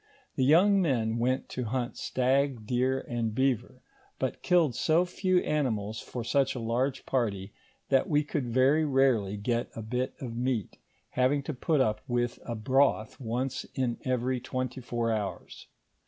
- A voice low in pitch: Yes, low, 130 Hz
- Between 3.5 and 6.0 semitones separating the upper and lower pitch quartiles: No, narrow, 2.6 semitones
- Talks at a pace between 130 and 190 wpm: Yes, average, 160 wpm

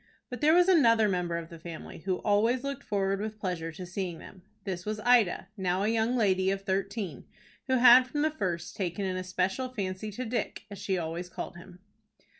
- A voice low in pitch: No, high, 195 Hz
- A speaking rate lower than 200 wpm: No, fast, 205 wpm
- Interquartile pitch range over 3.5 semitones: Yes, average, 4.1 semitones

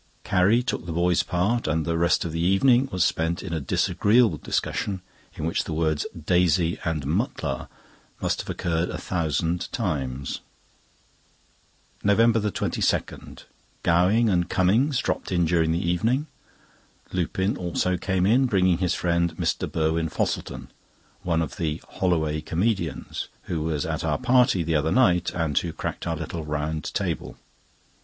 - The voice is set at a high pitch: No, very low, 85 Hz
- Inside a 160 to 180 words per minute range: No, average, 145 wpm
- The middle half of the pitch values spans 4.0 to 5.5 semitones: No, average, 2.9 semitones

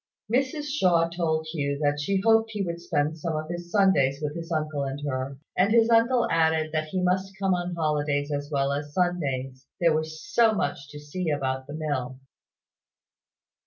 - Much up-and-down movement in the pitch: No, average, 4.1 semitones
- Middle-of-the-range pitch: Yes, medium, 160 Hz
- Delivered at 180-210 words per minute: Yes, average, 185 wpm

